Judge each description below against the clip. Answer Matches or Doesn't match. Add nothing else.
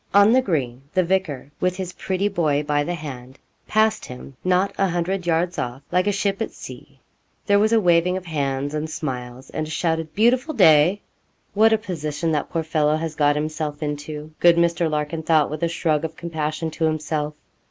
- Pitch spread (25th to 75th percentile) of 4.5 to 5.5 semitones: Doesn't match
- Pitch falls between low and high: Matches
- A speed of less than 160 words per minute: Doesn't match